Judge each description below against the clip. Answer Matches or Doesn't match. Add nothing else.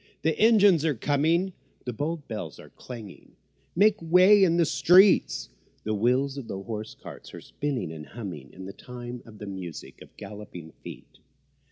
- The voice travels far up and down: Matches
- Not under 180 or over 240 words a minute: Doesn't match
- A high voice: Doesn't match